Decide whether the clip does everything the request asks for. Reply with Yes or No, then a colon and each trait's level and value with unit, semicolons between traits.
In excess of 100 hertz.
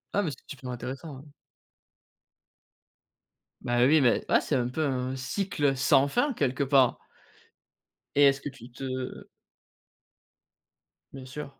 Yes: low, 135 Hz